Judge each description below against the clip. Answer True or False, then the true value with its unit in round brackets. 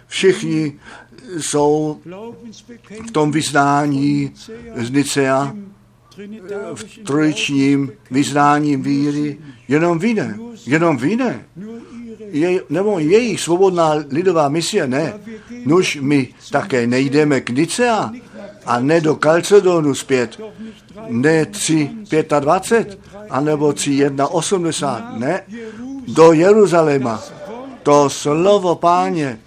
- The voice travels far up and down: True (6.3 semitones)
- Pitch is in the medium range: True (160 Hz)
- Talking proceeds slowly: True (90 wpm)